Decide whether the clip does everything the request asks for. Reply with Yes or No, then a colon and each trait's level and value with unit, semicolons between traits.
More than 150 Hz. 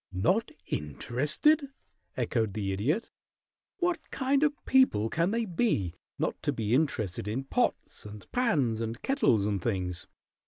No: low, 125 Hz